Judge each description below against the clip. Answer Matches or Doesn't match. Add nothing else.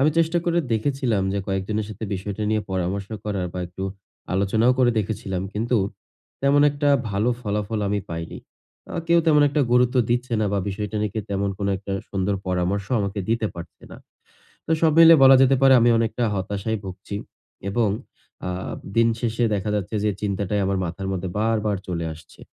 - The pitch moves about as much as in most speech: Matches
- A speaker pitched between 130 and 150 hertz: Doesn't match